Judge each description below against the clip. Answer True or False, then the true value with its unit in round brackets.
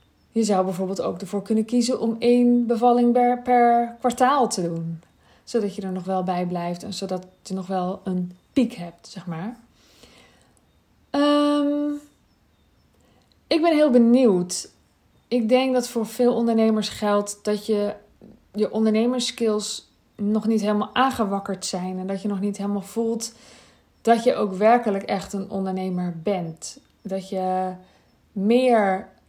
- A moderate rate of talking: True (145 wpm)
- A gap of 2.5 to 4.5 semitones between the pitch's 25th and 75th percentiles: True (4.0 semitones)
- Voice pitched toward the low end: False (210 Hz)